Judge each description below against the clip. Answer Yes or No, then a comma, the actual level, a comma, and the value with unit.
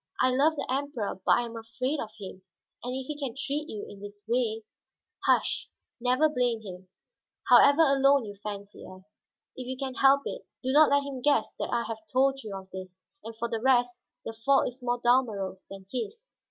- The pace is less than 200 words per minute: No, fast, 205 wpm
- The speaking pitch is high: Yes, high, 245 Hz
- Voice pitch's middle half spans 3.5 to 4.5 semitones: Yes, average, 4.0 semitones